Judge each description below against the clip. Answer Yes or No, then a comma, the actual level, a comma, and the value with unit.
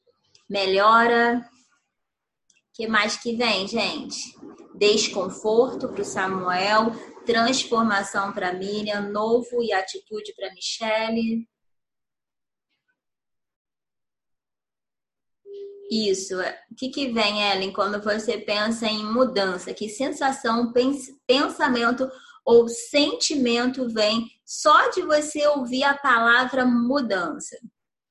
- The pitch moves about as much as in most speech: Yes, average, 4.0 semitones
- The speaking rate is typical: No, slow, 95 wpm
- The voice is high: Yes, high, 230 Hz